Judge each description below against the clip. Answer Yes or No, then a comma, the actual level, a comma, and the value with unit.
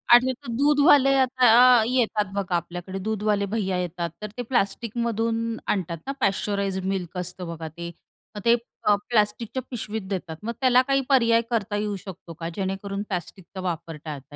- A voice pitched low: No, high, 205 Hz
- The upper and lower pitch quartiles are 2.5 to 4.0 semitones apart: No, average, 4.4 semitones